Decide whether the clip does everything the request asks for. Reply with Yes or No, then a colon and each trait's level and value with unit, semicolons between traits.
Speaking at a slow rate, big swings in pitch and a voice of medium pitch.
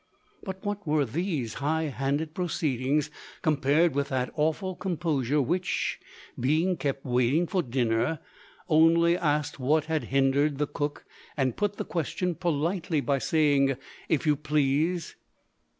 No: slow, 130 wpm; average, 3.5 semitones; medium, 150 Hz